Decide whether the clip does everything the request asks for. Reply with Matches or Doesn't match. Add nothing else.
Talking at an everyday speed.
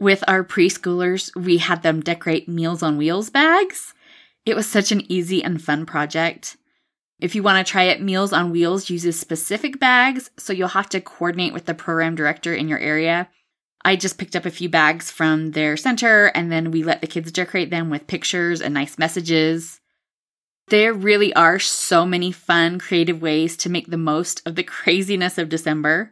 Matches